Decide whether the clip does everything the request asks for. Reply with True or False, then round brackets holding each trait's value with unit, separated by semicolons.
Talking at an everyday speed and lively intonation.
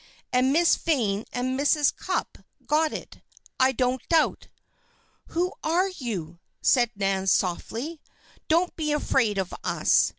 False (130 wpm; 6.5 semitones)